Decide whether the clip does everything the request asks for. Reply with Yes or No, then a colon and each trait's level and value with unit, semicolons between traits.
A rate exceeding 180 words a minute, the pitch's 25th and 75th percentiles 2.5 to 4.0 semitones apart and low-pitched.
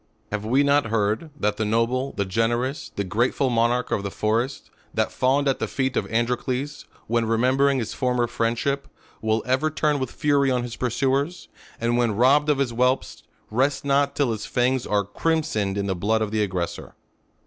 Yes: average, 190 wpm; average, 3.7 semitones; low, 125 Hz